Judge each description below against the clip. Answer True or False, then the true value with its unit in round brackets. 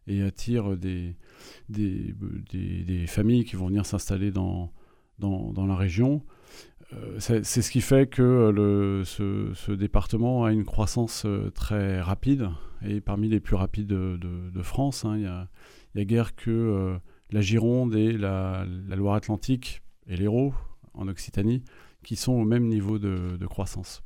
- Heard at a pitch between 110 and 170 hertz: False (100 Hz)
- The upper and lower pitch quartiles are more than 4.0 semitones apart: False (3.2 semitones)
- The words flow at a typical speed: True (170 wpm)